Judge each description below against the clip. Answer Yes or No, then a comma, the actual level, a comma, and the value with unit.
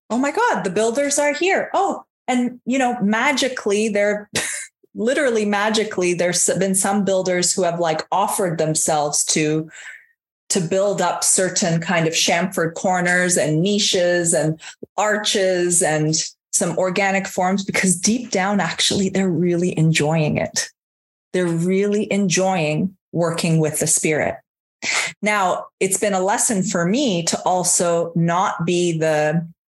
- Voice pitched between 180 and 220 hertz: Yes, medium, 185 Hz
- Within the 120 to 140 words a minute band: Yes, slow, 135 wpm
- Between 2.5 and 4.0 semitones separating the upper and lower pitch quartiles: Yes, average, 3.3 semitones